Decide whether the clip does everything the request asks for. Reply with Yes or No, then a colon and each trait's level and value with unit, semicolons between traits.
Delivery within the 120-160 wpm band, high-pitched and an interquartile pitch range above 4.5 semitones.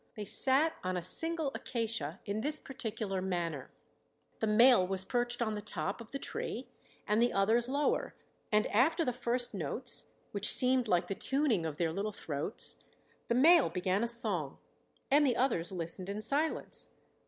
No: average, 170 wpm; high, 220 Hz; wide, 5.4 semitones